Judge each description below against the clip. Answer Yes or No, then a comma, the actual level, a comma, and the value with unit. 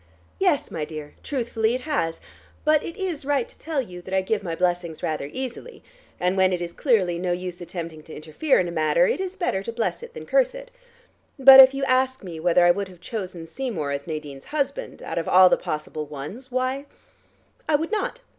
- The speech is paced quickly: Yes, fast, 215 wpm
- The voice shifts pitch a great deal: Yes, wide, 8.2 semitones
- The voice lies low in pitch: No, high, 190 Hz